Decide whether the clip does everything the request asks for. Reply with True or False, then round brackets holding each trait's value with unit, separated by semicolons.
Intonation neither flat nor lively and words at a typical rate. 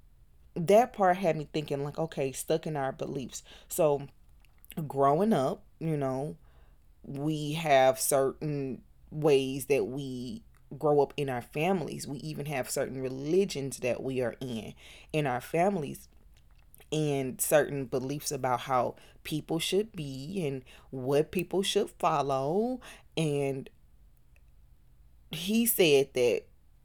False (4.3 semitones; 125 wpm)